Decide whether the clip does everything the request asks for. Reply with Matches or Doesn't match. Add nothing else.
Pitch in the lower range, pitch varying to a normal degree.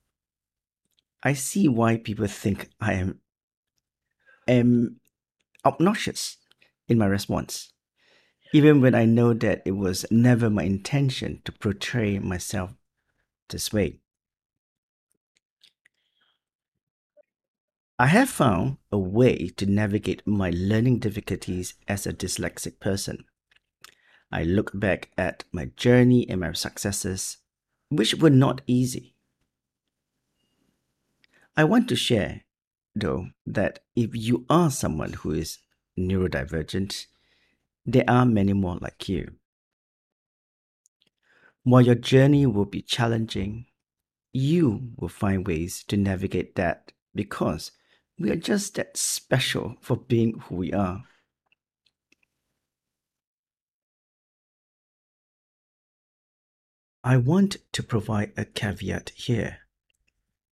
Doesn't match